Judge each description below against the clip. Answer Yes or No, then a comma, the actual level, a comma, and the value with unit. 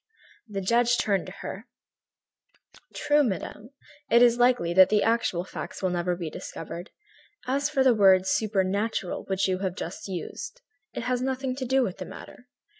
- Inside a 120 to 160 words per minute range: No, average, 170 wpm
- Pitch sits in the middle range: No, high, 210 Hz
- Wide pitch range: No, average, 4.8 semitones